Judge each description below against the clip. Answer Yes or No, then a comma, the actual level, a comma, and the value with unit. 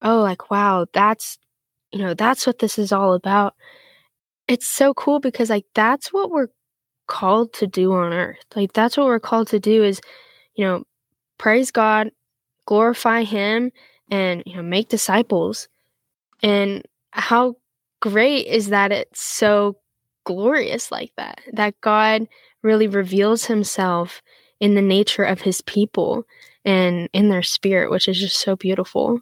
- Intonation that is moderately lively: Yes, average, 3.3 semitones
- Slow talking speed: No, average, 150 wpm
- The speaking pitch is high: Yes, high, 210 Hz